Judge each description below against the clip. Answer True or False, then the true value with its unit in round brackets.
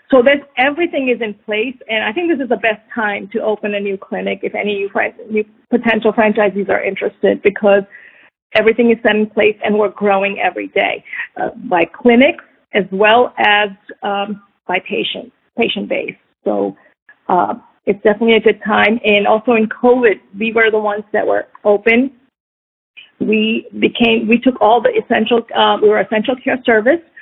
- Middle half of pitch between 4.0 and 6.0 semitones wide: False (2.7 semitones)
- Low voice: False (220 Hz)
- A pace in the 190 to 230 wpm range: False (175 wpm)